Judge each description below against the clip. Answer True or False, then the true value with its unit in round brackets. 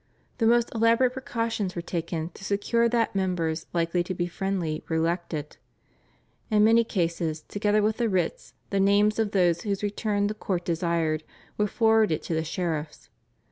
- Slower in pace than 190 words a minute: True (165 wpm)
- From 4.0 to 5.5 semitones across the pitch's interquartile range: True (4.4 semitones)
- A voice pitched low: False (195 Hz)